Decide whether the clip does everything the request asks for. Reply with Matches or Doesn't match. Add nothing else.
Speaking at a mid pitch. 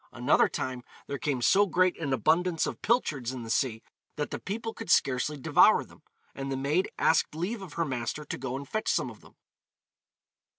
Matches